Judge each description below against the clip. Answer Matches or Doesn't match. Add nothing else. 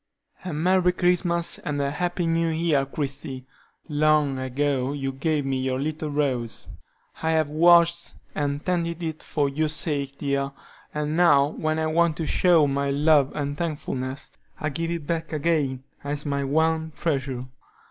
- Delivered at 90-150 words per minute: Doesn't match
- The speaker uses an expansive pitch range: Doesn't match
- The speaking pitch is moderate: Matches